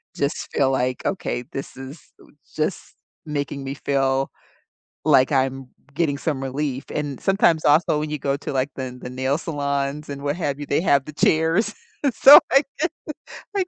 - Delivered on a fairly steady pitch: Yes, narrow, 2.3 semitones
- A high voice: No, medium, 140 Hz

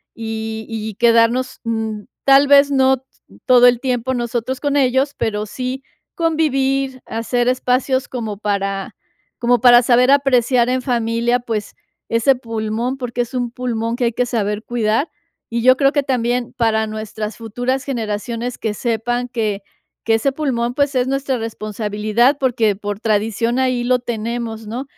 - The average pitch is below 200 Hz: No, high, 240 Hz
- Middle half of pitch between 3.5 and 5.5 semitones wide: No, narrow, 2.5 semitones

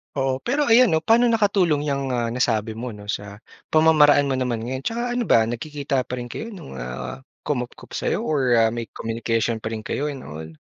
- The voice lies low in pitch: Yes, low, 130 Hz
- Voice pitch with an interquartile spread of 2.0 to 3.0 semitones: No, average, 5.2 semitones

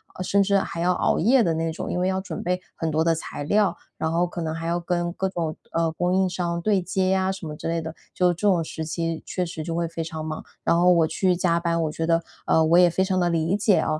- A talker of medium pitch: Yes, medium, 170 Hz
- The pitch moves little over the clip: Yes, narrow, 2.1 semitones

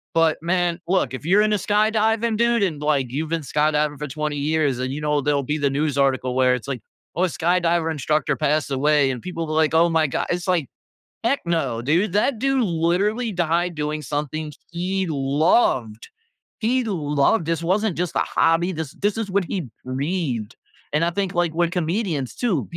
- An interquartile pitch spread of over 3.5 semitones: Yes, average, 4.1 semitones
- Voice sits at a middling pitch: Yes, medium, 160 Hz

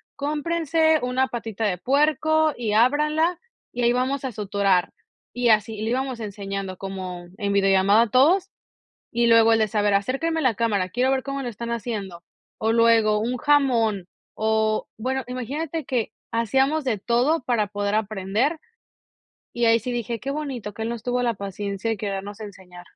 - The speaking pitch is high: Yes, high, 230 Hz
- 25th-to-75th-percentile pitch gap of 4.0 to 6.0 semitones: Yes, average, 4.4 semitones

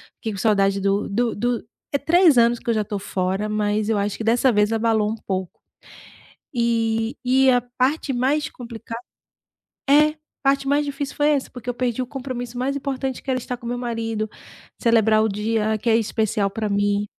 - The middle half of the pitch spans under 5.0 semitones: Yes, average, 3.3 semitones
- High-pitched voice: Yes, high, 230 Hz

